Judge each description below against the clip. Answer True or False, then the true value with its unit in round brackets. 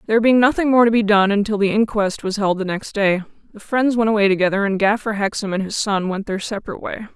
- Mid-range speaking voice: False (210 Hz)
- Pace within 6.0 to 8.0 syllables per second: True (6.3 syllables/s)